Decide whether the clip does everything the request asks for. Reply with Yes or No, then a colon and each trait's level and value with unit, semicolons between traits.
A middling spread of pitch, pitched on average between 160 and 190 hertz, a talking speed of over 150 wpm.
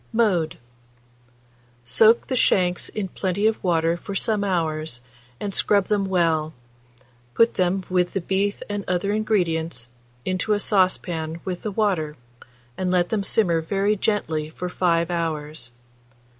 No: average, 3.7 semitones; medium, 185 Hz; average, 140 wpm